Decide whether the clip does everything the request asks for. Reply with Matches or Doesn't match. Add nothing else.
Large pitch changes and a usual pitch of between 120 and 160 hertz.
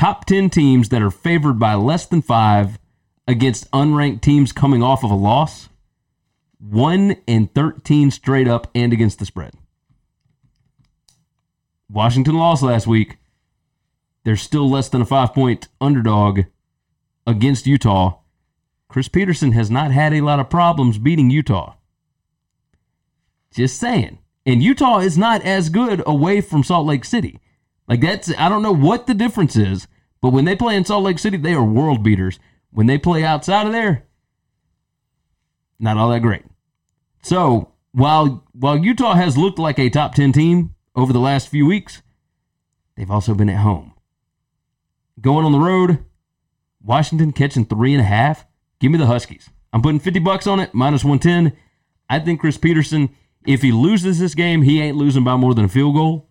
Matches